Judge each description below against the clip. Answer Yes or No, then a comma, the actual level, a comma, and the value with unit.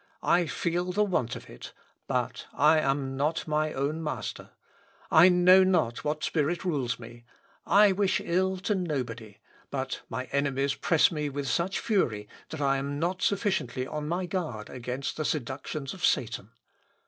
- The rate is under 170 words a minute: Yes, average, 160 wpm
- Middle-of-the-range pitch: Yes, medium, 150 Hz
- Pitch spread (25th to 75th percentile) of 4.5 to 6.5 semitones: Yes, average, 5.0 semitones